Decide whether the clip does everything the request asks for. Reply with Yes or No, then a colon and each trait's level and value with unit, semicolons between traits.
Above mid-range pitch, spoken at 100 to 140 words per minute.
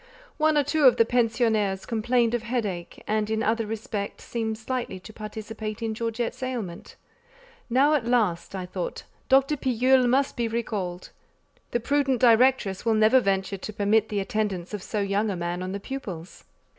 No: high, 220 Hz; average, 170 wpm